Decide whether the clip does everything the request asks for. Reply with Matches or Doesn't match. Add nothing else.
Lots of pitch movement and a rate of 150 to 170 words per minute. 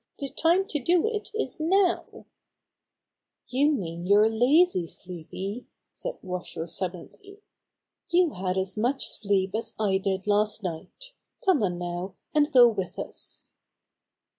Doesn't match